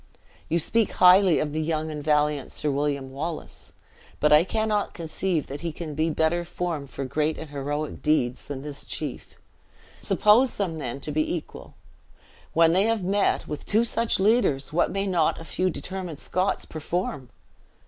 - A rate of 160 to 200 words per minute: Yes, average, 170 wpm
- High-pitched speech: No, medium, 160 Hz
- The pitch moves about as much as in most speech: Yes, average, 3.9 semitones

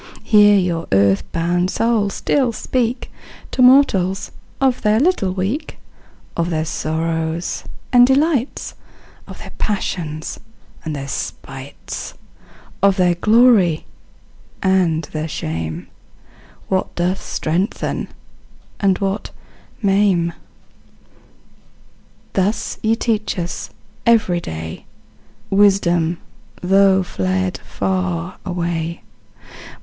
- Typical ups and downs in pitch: Yes, average, 4.0 semitones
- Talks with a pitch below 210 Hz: Yes, medium, 185 Hz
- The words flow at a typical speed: No, slow, 95 wpm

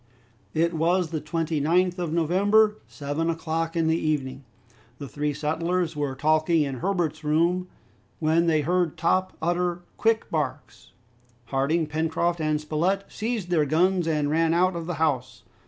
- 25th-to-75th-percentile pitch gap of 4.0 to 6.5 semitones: No, narrow, 2.6 semitones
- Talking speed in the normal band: Yes, average, 150 wpm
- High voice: No, medium, 165 Hz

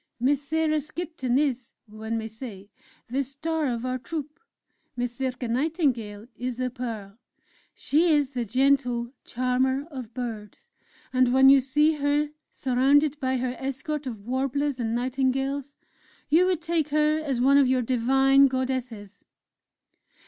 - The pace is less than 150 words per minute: Yes, average, 140 wpm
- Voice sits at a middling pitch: No, very high, 260 Hz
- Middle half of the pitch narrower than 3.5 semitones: Yes, average, 2.8 semitones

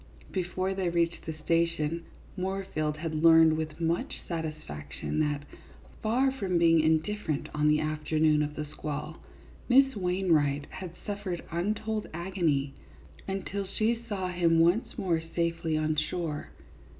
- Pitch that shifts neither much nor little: Yes, average, 3.6 semitones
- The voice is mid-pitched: Yes, medium, 165 Hz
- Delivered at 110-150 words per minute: Yes, slow, 135 wpm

